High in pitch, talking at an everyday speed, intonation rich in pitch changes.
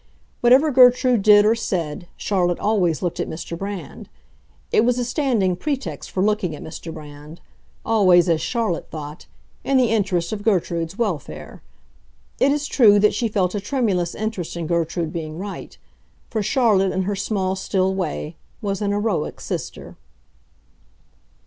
No: high, 195 Hz; average, 150 wpm; average, 4.5 semitones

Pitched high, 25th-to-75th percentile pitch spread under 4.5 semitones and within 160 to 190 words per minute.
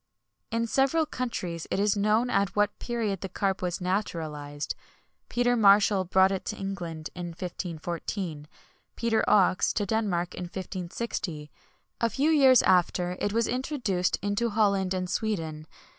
No: high, 195 Hz; average, 4.0 semitones; average, 150 wpm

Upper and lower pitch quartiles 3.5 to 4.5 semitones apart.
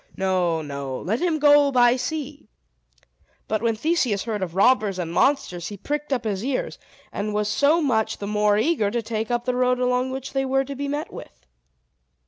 No: average, 5.2 semitones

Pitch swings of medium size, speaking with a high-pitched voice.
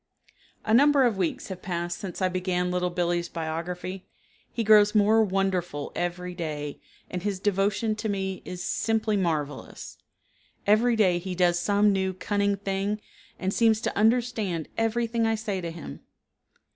Yes: average, 3.2 semitones; high, 195 Hz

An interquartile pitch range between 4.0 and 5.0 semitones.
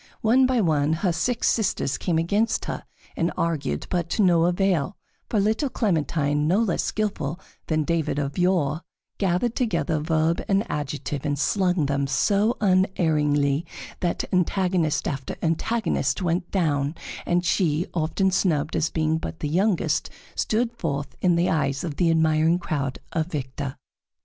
Yes: average, 4.3 semitones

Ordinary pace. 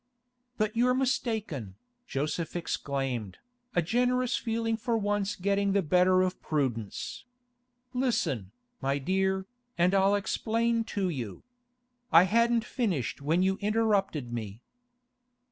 No: slow, 115 wpm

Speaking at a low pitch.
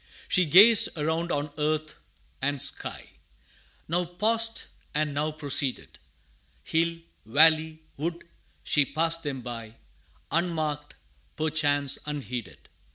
No: medium, 155 Hz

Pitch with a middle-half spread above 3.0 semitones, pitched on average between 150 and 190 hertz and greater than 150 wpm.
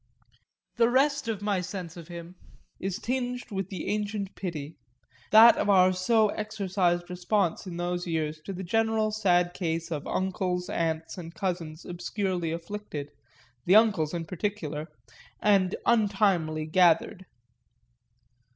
No: average, 3.6 semitones; medium, 185 Hz; slow, 135 wpm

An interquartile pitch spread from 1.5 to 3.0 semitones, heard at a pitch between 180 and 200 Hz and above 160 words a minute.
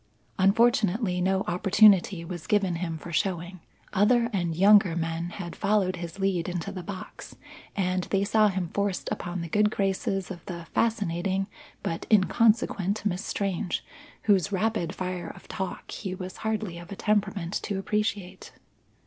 No: average, 2.7 semitones; high, 190 Hz; average, 150 wpm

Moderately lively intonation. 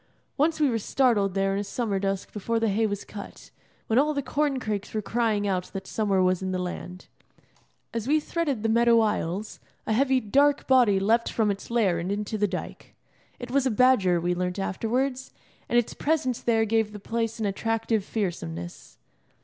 Yes: average, 3.8 semitones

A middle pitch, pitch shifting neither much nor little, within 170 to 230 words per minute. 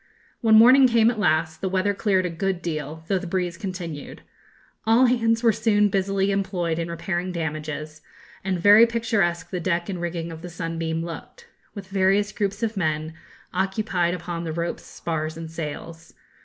Yes: medium, 180 Hz; average, 3.6 semitones; average, 175 wpm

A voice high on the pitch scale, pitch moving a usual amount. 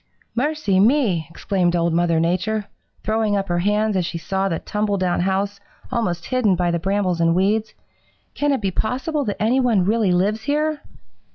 Yes: high, 200 Hz; average, 3.8 semitones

